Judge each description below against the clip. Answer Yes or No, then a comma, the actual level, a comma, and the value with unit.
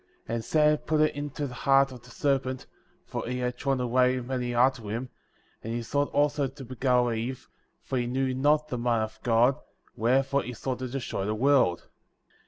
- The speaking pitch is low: Yes, low, 130 Hz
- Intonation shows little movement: Yes, narrow, 2.3 semitones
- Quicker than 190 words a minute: Yes, average, 200 wpm